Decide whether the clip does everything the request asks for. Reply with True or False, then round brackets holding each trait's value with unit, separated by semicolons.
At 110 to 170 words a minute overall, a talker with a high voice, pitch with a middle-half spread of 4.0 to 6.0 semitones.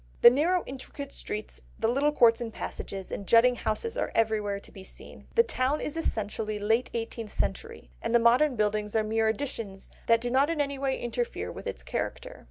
False (195 wpm; 235 Hz; 4.6 semitones)